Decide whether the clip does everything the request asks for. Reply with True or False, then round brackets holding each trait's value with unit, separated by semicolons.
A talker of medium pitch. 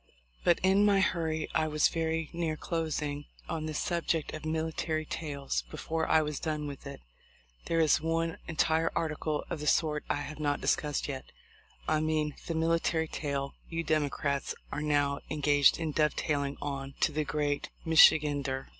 True (155 Hz)